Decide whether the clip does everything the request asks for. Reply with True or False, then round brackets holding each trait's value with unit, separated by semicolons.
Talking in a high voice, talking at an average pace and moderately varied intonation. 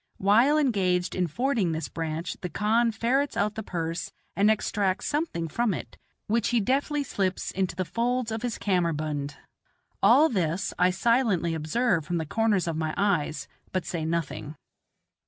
False (195 Hz; 160 wpm; 5.7 semitones)